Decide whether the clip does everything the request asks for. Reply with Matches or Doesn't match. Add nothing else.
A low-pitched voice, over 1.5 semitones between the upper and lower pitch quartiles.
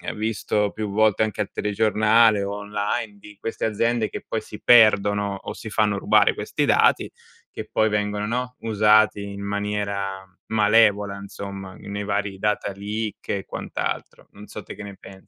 Doesn't match